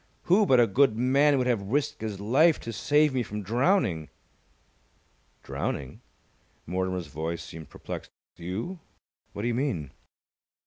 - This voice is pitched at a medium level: No, low, 115 Hz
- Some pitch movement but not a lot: No, wide, 7.2 semitones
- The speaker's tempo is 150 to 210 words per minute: No, average, 140 wpm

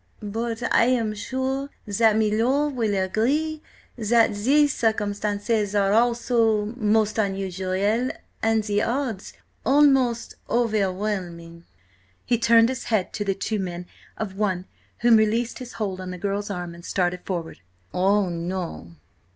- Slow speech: Yes, slow, 125 wpm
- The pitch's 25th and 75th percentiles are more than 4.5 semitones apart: No, average, 3.6 semitones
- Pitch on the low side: No, high, 215 Hz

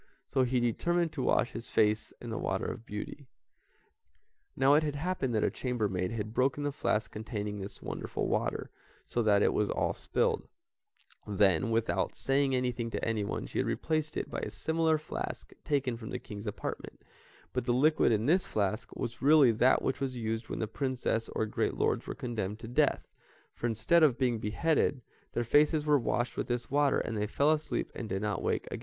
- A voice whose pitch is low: Yes, low, 120 Hz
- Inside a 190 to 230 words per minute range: Yes, average, 200 wpm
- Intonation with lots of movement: No, average, 4.8 semitones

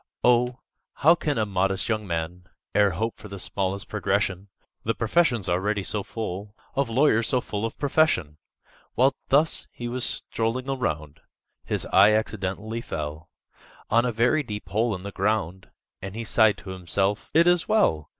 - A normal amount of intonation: Yes, average, 4.1 semitones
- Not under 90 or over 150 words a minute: No, average, 165 wpm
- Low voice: Yes, low, 105 Hz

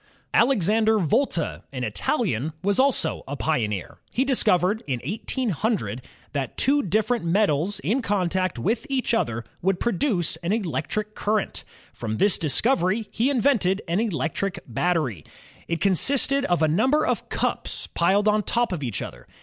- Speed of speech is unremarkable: Yes, average, 150 wpm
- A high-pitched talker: Yes, high, 195 Hz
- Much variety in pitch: Yes, wide, 6.1 semitones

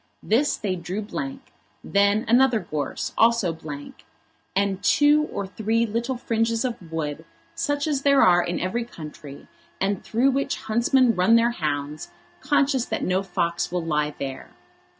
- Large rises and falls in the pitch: Yes, wide, 6.0 semitones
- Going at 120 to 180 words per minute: Yes, average, 150 wpm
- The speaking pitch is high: Yes, high, 210 Hz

